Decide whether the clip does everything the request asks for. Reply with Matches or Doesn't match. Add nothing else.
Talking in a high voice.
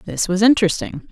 Matches